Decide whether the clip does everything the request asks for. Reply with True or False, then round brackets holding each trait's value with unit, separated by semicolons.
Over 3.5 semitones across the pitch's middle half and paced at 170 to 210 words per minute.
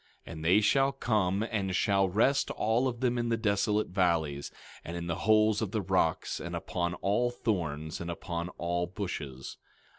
True (4.3 semitones; 180 wpm)